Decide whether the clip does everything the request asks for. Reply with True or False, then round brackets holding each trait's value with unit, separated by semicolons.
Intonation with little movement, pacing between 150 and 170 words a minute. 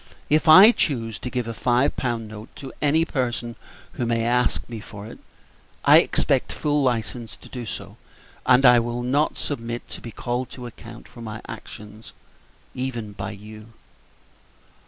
True (2.2 semitones; 165 wpm)